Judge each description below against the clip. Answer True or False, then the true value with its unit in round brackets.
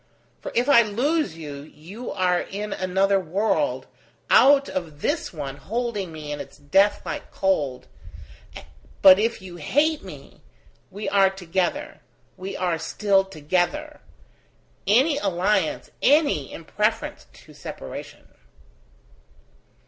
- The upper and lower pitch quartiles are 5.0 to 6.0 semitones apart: True (5.4 semitones)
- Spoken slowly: True (120 wpm)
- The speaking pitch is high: True (195 Hz)